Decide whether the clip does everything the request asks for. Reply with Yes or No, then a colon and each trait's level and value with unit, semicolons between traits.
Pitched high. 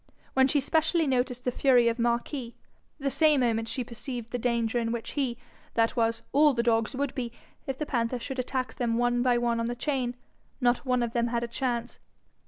Yes: high, 245 Hz